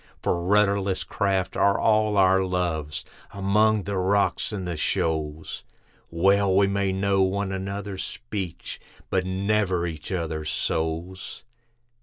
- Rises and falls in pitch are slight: Yes, narrow, 2.3 semitones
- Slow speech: Yes, slow, 125 wpm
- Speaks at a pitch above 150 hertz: No, very low, 95 Hz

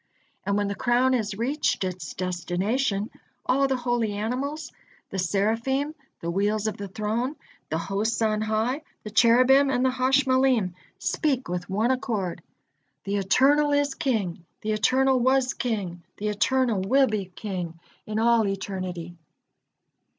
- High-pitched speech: Yes, high, 220 Hz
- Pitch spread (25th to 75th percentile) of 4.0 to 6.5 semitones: Yes, average, 4.9 semitones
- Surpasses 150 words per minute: No, average, 145 wpm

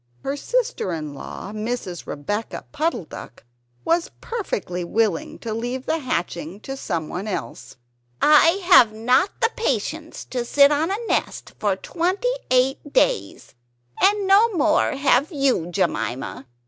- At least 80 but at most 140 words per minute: Yes, slow, 135 wpm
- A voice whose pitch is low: No, very high, 255 Hz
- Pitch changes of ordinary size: No, wide, 8.9 semitones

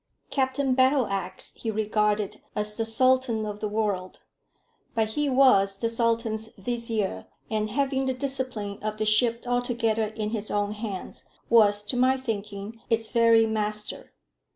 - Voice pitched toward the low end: No, high, 220 Hz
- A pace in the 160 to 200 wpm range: No, average, 145 wpm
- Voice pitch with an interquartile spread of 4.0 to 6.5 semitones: No, average, 2.7 semitones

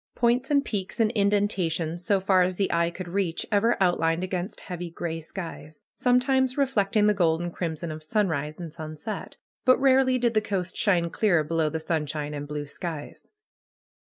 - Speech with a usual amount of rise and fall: Yes, average, 4.6 semitones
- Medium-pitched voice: Yes, medium, 180 Hz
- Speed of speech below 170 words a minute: No, average, 175 wpm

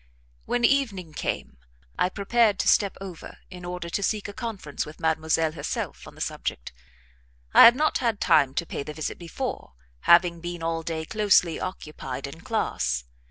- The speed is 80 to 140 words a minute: No, average, 170 wpm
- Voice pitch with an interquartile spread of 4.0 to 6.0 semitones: Yes, average, 4.3 semitones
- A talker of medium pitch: Yes, medium, 175 Hz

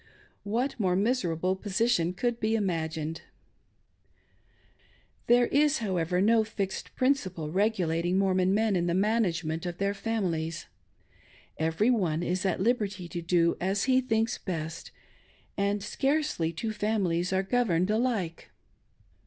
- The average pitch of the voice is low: No, high, 195 Hz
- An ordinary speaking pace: No, slow, 130 wpm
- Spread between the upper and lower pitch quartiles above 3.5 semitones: Yes, average, 4.6 semitones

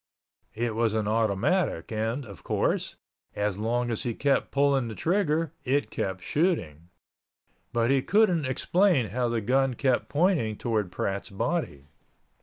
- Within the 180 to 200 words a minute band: No, average, 145 wpm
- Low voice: Yes, low, 120 Hz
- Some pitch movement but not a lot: Yes, average, 5.0 semitones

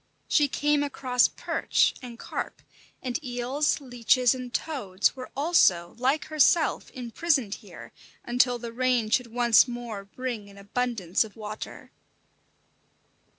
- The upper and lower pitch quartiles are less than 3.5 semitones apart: Yes, average, 2.9 semitones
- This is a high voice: Yes, high, 245 Hz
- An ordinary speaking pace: No, slow, 125 wpm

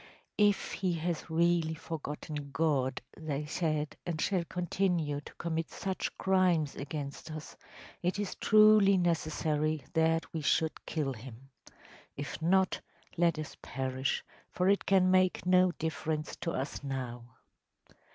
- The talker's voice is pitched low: No, medium, 160 Hz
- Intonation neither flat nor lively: Yes, average, 3.5 semitones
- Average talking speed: No, slow, 130 wpm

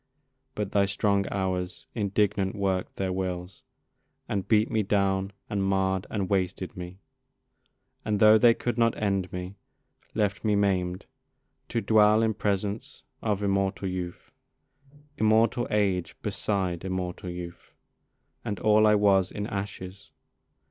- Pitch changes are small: Yes, narrow, 2.1 semitones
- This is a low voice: Yes, low, 100 Hz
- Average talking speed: No, slow, 130 wpm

